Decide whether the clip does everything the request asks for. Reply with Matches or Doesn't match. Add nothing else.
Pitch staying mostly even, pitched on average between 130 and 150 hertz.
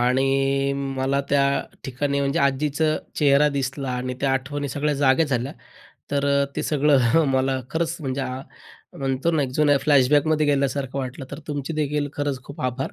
Matches